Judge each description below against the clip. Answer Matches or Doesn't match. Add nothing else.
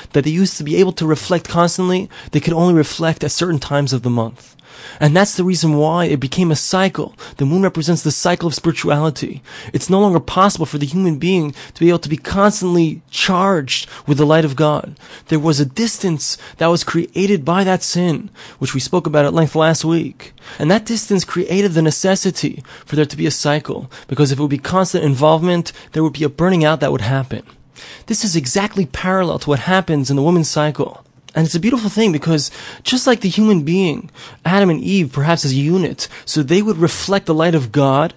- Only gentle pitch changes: Doesn't match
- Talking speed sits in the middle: Doesn't match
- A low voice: Doesn't match